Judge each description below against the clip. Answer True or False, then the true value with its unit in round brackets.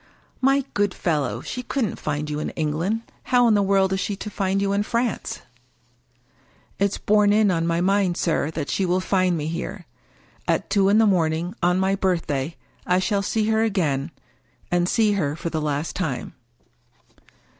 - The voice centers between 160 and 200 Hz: True (190 Hz)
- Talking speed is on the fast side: False (190 wpm)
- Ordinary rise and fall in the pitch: True (3.8 semitones)